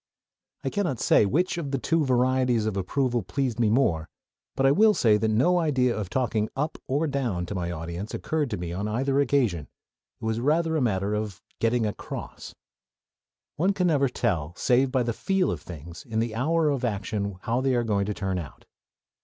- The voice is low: Yes, low, 120 Hz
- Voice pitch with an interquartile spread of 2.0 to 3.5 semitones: No, average, 5.1 semitones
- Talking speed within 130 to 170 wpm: No, average, 200 wpm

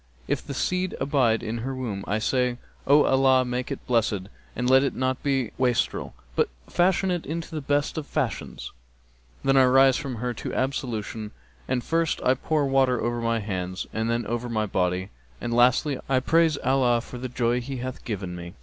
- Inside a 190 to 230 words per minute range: Yes, average, 195 wpm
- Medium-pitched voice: No, low, 125 Hz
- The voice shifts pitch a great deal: No, average, 3.3 semitones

